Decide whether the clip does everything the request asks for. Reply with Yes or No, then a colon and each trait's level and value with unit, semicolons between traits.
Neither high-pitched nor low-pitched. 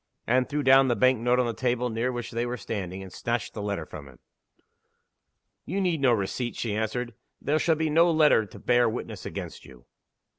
No: low, 120 Hz